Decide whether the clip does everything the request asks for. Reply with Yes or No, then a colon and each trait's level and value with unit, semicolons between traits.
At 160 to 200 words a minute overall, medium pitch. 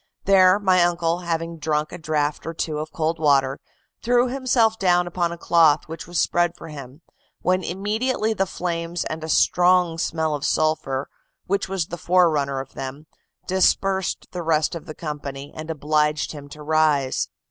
Yes: average, 170 wpm; medium, 165 Hz